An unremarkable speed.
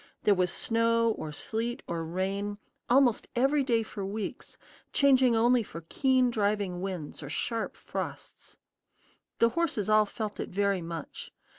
Yes: average, 145 wpm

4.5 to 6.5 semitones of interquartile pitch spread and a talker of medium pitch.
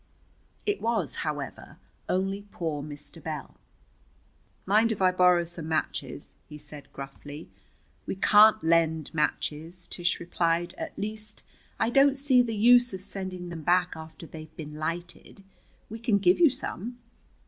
Yes: average, 5.1 semitones; medium, 175 Hz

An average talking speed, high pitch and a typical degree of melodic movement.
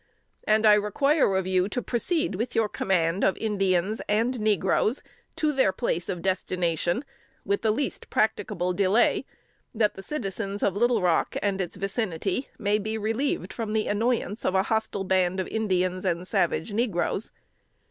Yes: average, 160 wpm; high, 205 Hz; average, 3.1 semitones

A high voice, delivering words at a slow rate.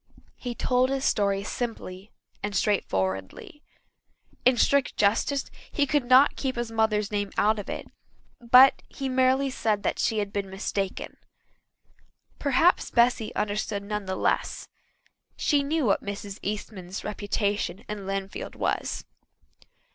Yes: high, 215 Hz; slow, 130 wpm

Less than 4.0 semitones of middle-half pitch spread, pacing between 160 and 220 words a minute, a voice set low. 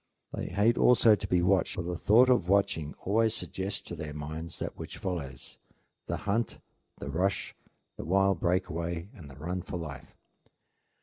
Yes: average, 3.6 semitones; average, 175 wpm; very low, 90 Hz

